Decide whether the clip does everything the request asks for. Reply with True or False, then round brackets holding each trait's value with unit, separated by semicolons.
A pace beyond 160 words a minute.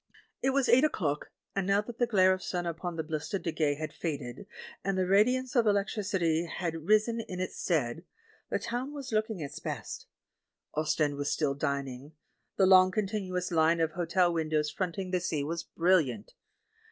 True (175 wpm)